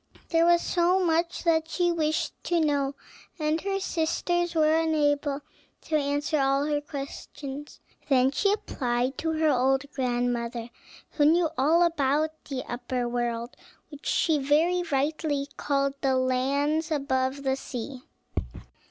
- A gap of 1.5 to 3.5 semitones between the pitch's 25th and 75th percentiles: Yes, average, 3.2 semitones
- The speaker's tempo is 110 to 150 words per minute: Yes, slow, 135 wpm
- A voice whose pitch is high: Yes, very high, 290 Hz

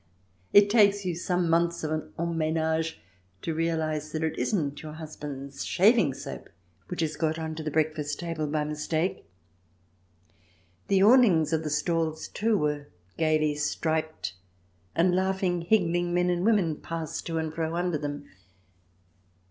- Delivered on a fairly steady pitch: Yes, narrow, 2.3 semitones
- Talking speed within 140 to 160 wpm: Yes, average, 150 wpm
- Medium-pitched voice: Yes, medium, 160 Hz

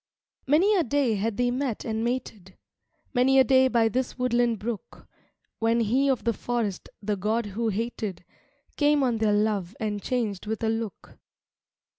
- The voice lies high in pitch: Yes, high, 230 Hz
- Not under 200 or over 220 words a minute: No, average, 170 wpm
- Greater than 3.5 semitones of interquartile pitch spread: No, average, 2.9 semitones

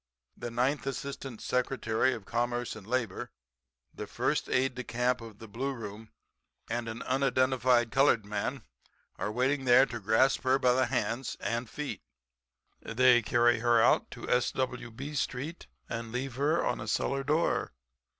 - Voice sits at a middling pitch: No, low, 125 Hz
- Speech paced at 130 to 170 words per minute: Yes, average, 160 wpm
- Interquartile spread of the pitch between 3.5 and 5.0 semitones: No, narrow, 2.4 semitones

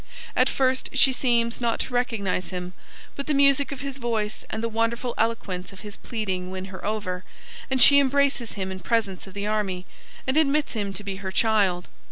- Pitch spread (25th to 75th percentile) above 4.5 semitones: Yes, average, 5.2 semitones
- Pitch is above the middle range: Yes, high, 220 Hz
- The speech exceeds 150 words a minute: Yes, average, 200 wpm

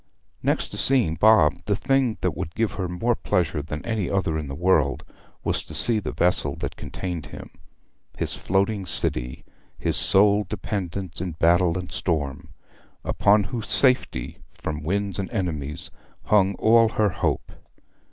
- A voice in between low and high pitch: No, very low, 95 Hz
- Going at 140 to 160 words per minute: Yes, average, 155 wpm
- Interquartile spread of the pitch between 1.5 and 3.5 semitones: No, average, 4.7 semitones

